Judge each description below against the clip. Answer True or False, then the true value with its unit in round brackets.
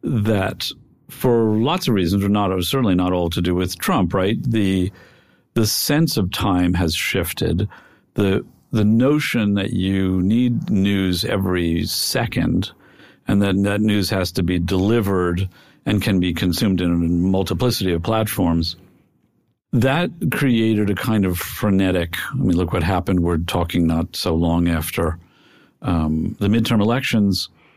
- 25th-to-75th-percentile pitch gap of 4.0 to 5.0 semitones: False (3.4 semitones)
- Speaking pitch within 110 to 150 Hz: False (95 Hz)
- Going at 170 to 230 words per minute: False (150 wpm)